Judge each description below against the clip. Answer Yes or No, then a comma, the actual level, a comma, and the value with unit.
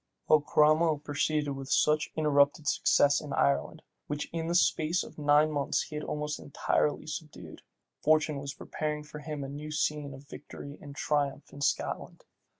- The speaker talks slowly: No, average, 165 wpm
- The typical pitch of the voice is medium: Yes, medium, 150 Hz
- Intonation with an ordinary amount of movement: No, narrow, 1.3 semitones